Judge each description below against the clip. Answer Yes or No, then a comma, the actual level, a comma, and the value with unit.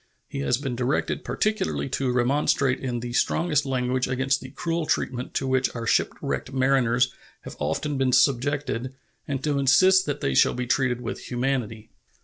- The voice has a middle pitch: No, low, 130 Hz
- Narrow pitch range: Yes, narrow, 2.1 semitones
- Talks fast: No, average, 165 wpm